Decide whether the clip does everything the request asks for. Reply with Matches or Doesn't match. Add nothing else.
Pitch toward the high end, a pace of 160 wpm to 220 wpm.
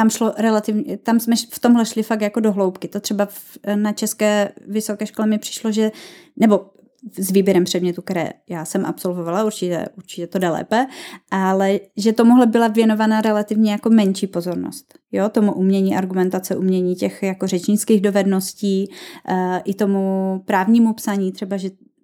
Matches